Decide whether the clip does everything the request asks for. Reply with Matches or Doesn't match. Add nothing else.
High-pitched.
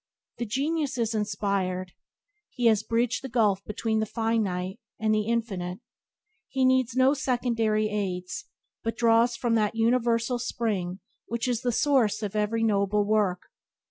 Matches